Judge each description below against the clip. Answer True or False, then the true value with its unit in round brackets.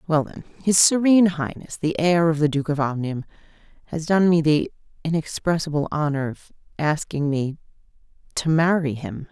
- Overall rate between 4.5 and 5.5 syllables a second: True (5.2 syllables/s)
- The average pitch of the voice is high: False (155 Hz)